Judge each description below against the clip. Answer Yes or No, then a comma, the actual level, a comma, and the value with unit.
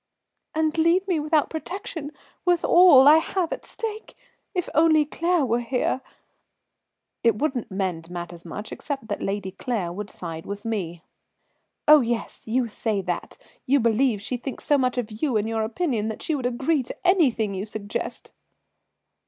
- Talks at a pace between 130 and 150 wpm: No, average, 165 wpm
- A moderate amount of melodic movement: No, wide, 6.8 semitones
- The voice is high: Yes, high, 245 Hz